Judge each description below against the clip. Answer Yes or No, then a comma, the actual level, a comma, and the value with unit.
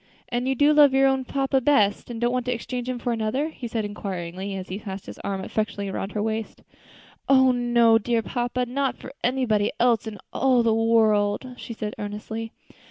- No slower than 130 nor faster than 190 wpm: No, average, 200 wpm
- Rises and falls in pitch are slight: No, average, 3.2 semitones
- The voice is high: Yes, high, 230 Hz